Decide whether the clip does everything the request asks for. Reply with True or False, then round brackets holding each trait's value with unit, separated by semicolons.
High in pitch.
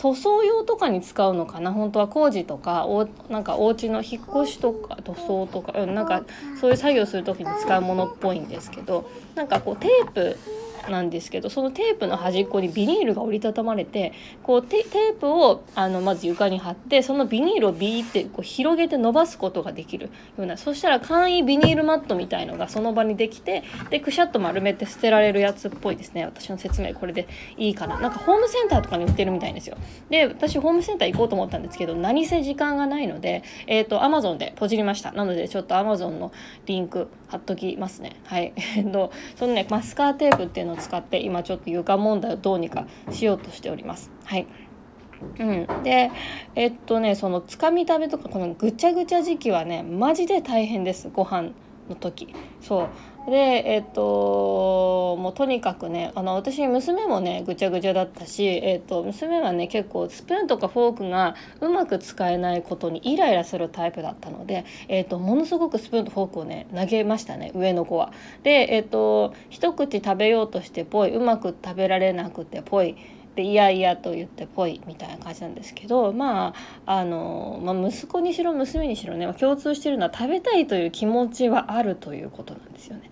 True (215 Hz)